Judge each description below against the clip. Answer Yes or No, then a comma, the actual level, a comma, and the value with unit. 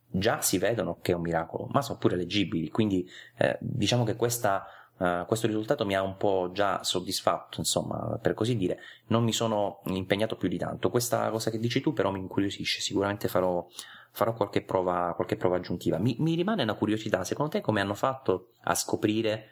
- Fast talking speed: Yes, fast, 195 wpm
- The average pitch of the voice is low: Yes, low, 100 Hz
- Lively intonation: No, average, 3.6 semitones